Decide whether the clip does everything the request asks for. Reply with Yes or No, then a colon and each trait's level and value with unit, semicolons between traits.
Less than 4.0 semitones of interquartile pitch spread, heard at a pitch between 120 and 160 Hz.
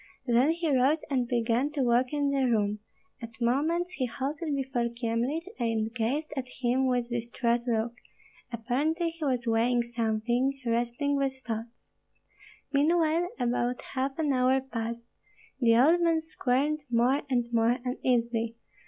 No: average, 3.2 semitones; very high, 250 Hz